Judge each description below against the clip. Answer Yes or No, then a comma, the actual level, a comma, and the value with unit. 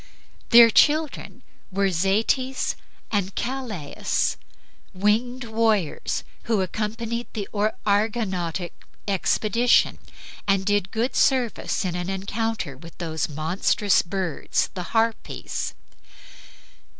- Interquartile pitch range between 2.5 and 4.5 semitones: Yes, average, 3.6 semitones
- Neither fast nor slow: No, slow, 90 wpm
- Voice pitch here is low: No, high, 205 Hz